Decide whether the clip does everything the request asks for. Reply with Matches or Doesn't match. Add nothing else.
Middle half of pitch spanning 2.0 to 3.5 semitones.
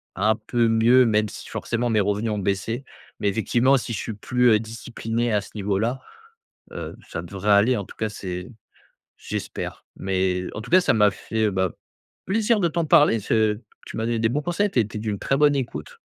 Matches